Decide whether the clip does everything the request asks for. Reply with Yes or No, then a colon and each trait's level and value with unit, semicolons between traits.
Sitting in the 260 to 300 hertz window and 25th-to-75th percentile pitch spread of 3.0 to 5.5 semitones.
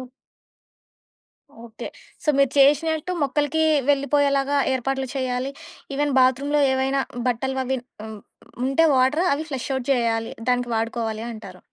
No: very high, 265 Hz; narrow, 2.5 semitones